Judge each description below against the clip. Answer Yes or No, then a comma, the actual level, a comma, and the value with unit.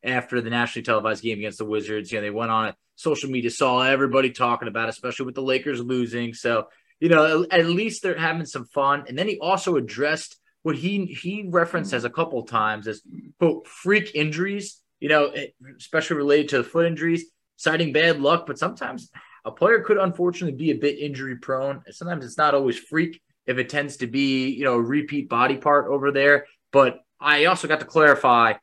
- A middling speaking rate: No, fast, 210 wpm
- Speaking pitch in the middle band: Yes, medium, 145 Hz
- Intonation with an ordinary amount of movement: Yes, average, 4.8 semitones